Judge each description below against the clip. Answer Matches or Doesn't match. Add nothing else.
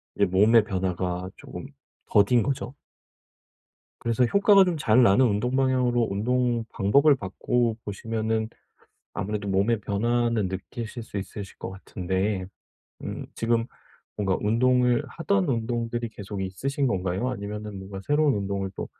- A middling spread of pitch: Matches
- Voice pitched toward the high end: Doesn't match